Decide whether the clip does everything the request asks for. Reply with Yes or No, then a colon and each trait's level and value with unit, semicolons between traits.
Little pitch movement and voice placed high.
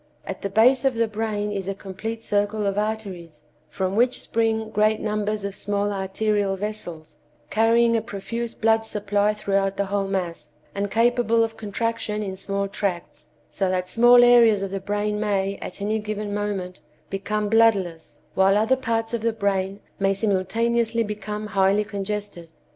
Yes: narrow, 2.2 semitones; high, 210 Hz